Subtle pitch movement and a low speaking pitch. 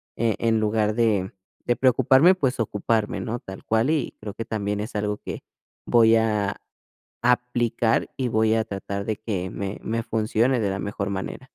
Yes: narrow, 2.3 semitones; low, 110 Hz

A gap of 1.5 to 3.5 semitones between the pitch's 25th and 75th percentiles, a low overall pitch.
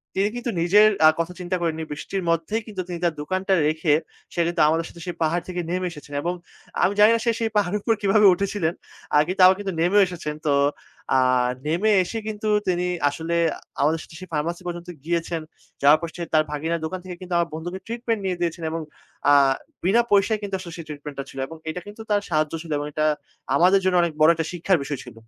No: average, 3.2 semitones; medium, 175 Hz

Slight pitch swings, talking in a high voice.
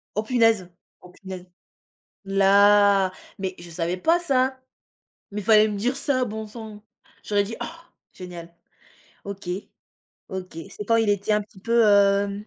No: average, 3.0 semitones; high, 205 Hz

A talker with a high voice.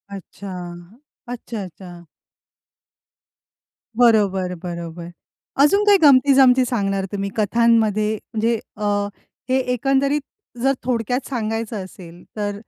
Yes: high, 220 Hz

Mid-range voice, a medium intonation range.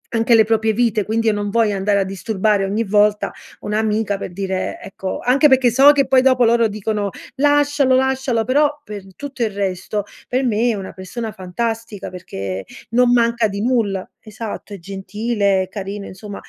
No: high, 220 Hz; average, 3.4 semitones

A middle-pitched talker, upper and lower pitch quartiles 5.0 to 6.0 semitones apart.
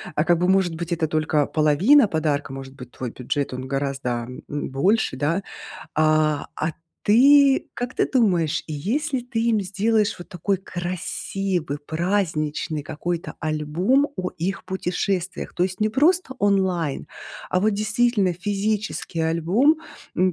Yes: medium, 180 Hz; average, 5.3 semitones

